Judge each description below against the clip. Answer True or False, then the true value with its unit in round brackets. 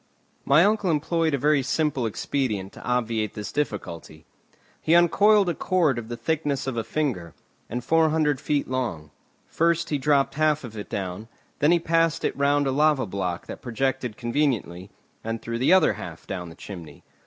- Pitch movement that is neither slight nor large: False (5.9 semitones)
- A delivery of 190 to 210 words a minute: False (180 wpm)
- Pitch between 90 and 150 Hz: True (135 Hz)